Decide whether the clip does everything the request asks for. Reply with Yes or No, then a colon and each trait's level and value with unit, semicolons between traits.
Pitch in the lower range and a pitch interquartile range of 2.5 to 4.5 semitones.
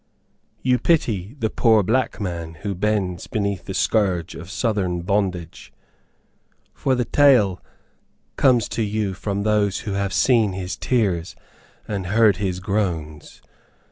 Yes: low, 100 Hz; average, 3.3 semitones